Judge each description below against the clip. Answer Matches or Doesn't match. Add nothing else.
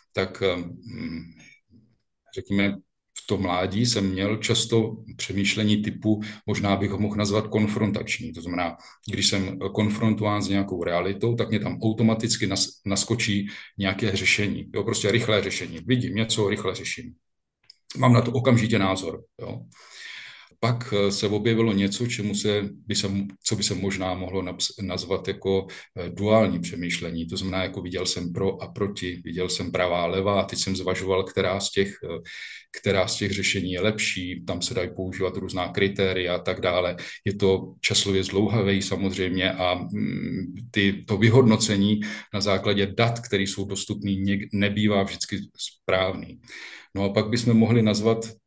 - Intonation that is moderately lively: Doesn't match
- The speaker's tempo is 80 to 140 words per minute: Doesn't match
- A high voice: Doesn't match